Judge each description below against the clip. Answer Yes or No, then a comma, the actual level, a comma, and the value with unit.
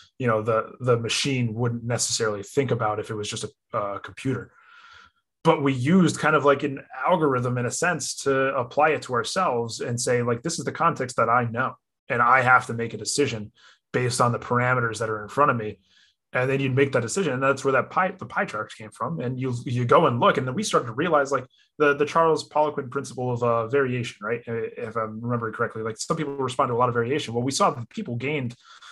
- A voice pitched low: Yes, low, 125 Hz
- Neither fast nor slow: No, fast, 240 wpm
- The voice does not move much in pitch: No, average, 3.5 semitones